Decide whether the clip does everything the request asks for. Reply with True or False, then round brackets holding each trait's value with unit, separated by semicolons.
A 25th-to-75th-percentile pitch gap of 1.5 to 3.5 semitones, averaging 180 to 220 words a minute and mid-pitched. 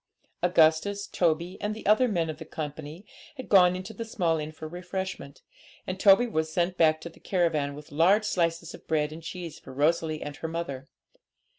True (3.1 semitones; 190 wpm; 170 Hz)